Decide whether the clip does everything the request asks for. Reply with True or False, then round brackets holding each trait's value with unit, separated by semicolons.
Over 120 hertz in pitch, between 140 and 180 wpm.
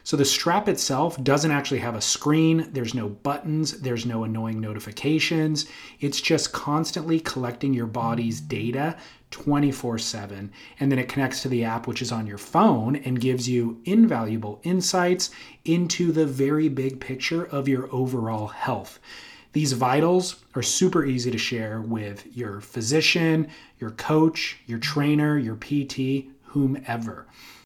True (135 Hz; 145 wpm)